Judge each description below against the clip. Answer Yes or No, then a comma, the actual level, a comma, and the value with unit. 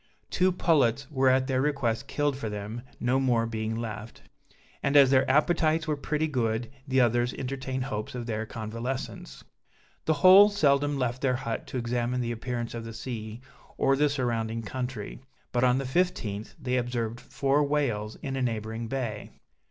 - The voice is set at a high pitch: No, low, 125 Hz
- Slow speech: No, average, 170 wpm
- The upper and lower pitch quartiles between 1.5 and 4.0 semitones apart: Yes, average, 3.2 semitones